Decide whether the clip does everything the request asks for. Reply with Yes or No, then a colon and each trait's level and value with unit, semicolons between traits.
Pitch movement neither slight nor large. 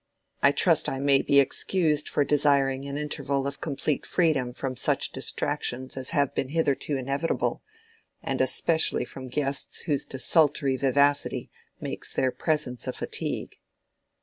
No: narrow, 1.8 semitones